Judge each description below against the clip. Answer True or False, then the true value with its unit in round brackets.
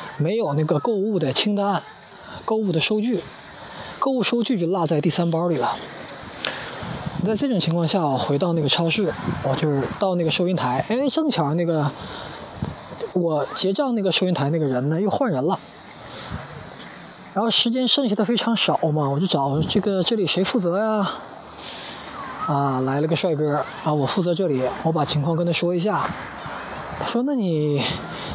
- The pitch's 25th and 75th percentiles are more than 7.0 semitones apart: False (5.5 semitones)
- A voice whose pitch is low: False (175 Hz)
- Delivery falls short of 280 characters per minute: True (245 characters per minute)